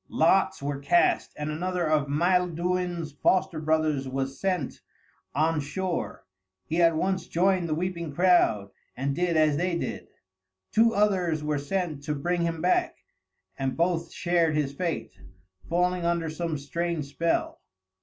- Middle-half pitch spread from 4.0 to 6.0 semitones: No, average, 3.0 semitones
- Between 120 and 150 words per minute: Yes, average, 145 wpm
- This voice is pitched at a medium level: Yes, medium, 165 Hz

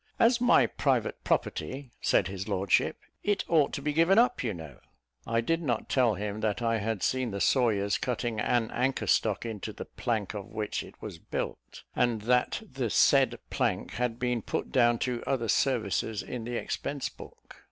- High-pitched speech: No, low, 120 Hz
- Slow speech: No, average, 185 wpm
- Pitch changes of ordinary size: Yes, average, 3.4 semitones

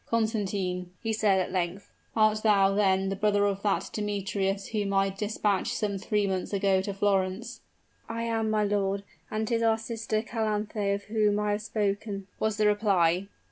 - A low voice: No, high, 205 Hz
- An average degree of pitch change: No, narrow, 1.8 semitones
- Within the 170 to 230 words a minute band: Yes, average, 175 wpm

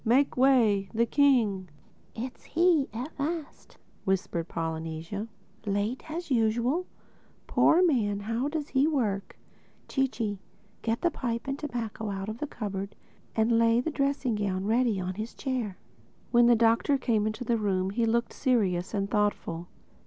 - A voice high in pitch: Yes, high, 230 Hz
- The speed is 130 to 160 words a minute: Yes, average, 140 wpm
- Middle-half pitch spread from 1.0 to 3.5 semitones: No, average, 4.6 semitones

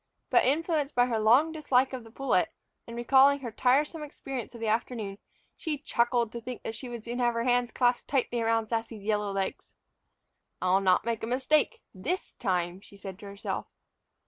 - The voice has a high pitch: Yes, high, 235 Hz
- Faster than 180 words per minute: Yes, average, 190 wpm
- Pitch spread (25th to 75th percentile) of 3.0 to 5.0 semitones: Yes, average, 3.4 semitones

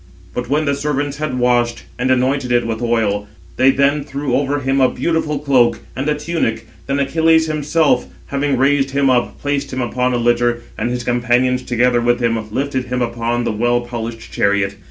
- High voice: No, low, 125 Hz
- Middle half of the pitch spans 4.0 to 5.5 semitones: No, average, 2.8 semitones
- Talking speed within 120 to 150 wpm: No, average, 190 wpm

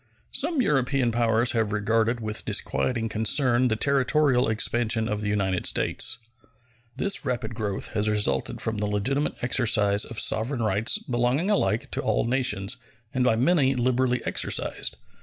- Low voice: Yes, low, 120 Hz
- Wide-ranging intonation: No, average, 3.0 semitones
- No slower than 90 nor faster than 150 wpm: Yes, average, 145 wpm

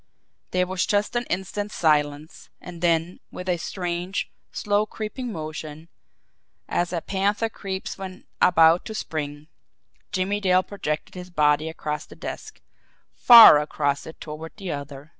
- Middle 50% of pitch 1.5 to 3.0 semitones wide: No, average, 4.1 semitones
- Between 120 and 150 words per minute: Yes, average, 140 wpm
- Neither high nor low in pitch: Yes, medium, 175 Hz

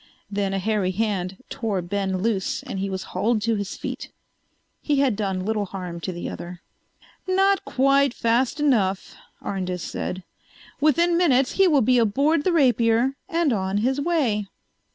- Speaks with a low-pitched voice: No, high, 225 Hz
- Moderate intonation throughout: No, wide, 6.3 semitones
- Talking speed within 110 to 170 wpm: Yes, average, 160 wpm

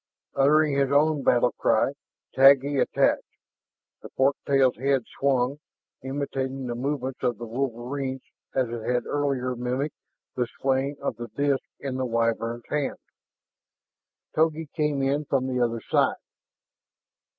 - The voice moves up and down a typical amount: No, narrow, 2.3 semitones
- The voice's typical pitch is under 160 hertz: Yes, low, 135 Hz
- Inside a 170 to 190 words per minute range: No, slow, 135 wpm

